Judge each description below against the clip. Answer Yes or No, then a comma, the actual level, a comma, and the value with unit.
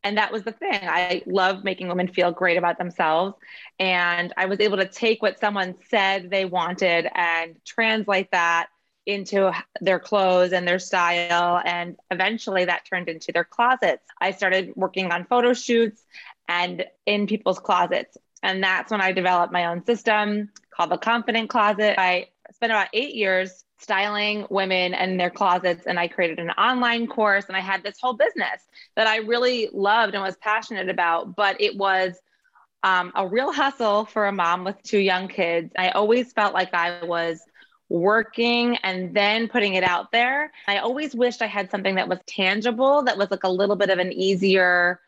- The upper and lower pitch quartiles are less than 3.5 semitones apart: Yes, average, 3.1 semitones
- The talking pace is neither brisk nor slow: Yes, average, 180 wpm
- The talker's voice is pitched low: No, high, 195 Hz